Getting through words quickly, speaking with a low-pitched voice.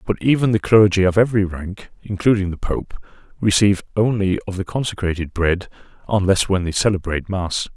No: average, 160 wpm; low, 100 Hz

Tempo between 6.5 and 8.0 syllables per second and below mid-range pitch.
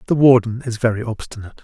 Yes: 7.4 syllables/s; low, 115 Hz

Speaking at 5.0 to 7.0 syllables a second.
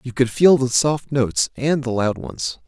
No: 4.5 syllables/s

